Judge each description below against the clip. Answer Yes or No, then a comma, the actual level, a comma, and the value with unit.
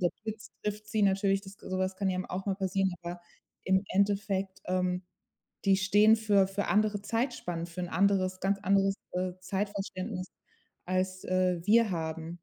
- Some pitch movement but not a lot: No, narrow, 1.6 semitones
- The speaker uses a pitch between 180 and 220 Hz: Yes, high, 190 Hz